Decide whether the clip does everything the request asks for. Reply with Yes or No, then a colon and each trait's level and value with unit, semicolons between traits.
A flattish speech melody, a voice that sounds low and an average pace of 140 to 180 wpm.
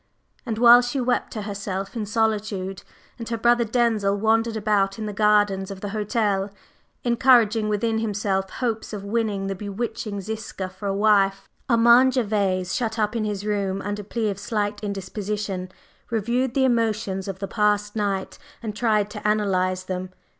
No: narrow, 2.3 semitones; high, 210 Hz; average, 165 wpm